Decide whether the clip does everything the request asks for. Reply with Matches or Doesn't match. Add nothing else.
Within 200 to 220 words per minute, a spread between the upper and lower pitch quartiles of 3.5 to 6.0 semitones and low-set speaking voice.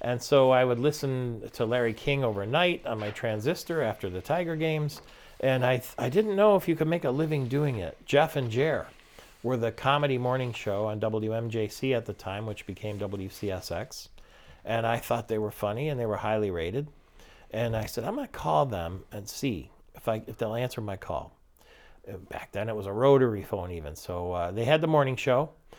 Matches